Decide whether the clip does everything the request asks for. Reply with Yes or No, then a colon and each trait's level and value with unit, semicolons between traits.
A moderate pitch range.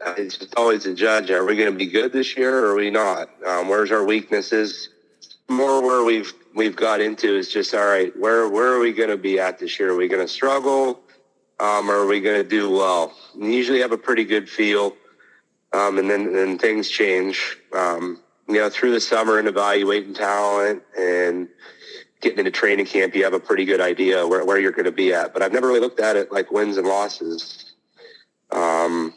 Yes: average, 4.7 semitones